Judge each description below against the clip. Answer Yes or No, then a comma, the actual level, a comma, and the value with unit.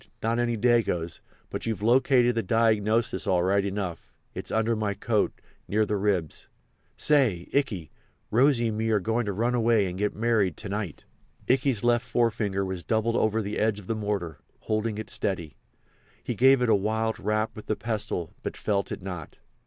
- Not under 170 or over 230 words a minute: Yes, average, 175 wpm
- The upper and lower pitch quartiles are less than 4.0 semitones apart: Yes, average, 2.8 semitones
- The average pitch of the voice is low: Yes, low, 110 Hz